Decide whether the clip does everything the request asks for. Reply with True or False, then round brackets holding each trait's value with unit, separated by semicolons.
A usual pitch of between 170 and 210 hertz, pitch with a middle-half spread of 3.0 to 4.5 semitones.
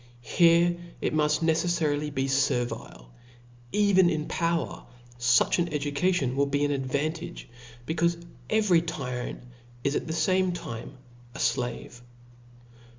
False (150 Hz; 4.2 semitones)